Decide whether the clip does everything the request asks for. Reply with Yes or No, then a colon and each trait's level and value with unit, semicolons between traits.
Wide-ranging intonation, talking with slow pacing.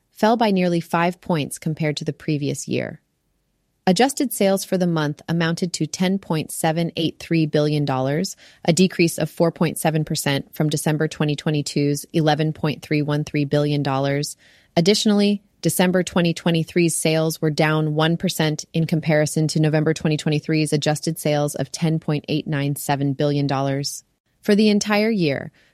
No: narrow, 2.4 semitones; slow, 115 wpm